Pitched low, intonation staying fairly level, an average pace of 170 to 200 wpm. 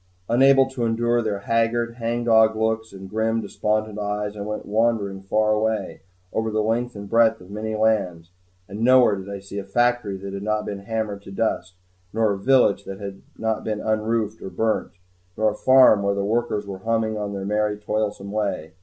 Yes: low, 110 Hz; narrow, 2.0 semitones; average, 195 wpm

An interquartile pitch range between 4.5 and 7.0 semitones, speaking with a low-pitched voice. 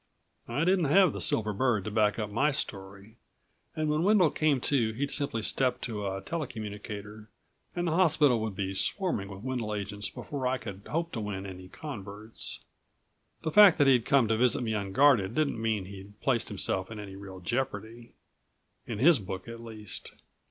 Yes: wide, 5.5 semitones; low, 110 Hz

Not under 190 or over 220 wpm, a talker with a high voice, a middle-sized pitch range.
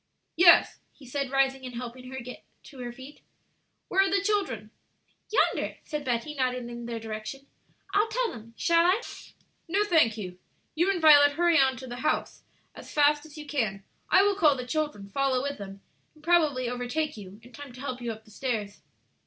Yes: average, 200 wpm; very high, 270 Hz; average, 4.6 semitones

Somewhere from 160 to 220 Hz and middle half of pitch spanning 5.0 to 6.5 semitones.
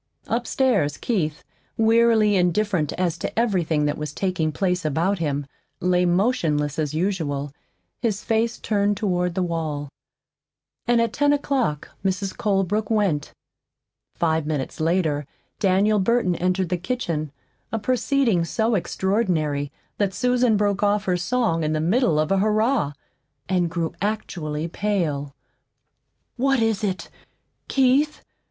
Yes: medium, 185 Hz; wide, 5.5 semitones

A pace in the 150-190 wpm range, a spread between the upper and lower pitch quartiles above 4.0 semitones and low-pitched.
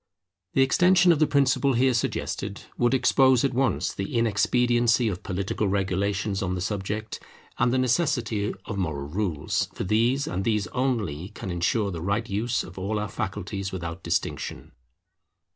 Yes: average, 160 wpm; average, 4.5 semitones; low, 105 Hz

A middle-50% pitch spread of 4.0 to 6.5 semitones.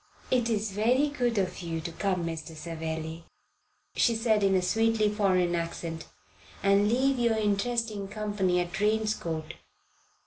Yes: average, 4.6 semitones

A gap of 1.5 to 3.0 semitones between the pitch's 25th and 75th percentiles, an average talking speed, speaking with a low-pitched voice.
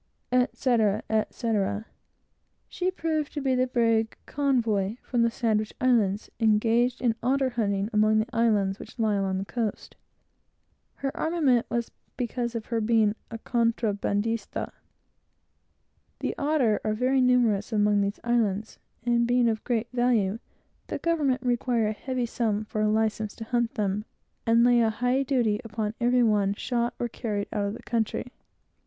No: narrow, 2.6 semitones; average, 155 wpm; high, 230 Hz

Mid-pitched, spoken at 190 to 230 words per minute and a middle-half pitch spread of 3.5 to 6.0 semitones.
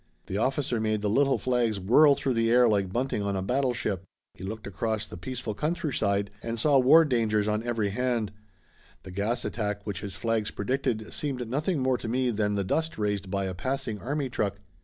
No: low, 115 Hz; average, 200 wpm; average, 4.0 semitones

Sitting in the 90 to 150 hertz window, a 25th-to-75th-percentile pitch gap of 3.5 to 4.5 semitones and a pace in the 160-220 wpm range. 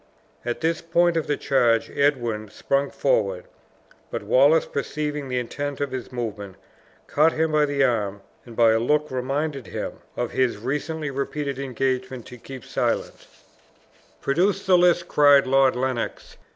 No: medium, 140 Hz; average, 3.8 semitones; average, 150 wpm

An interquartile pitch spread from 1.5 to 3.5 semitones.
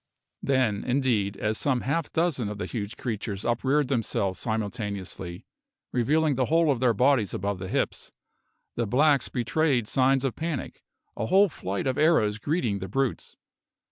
No: average, 5.1 semitones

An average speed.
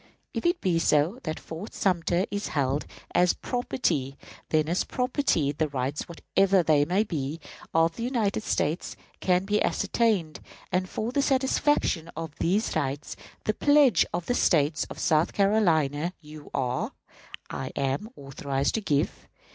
Yes: average, 150 wpm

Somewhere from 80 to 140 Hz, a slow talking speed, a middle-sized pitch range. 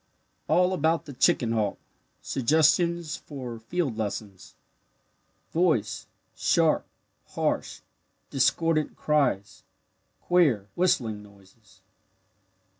No: low, 135 Hz; slow, 80 wpm; wide, 7.2 semitones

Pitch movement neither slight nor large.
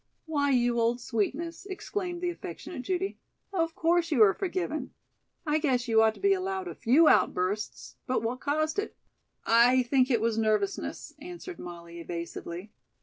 No: wide, 7.5 semitones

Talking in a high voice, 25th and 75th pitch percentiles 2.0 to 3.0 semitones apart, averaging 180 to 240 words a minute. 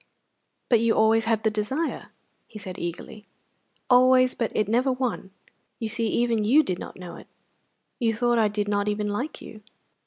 Yes: high, 225 Hz; narrow, 2.6 semitones; average, 185 wpm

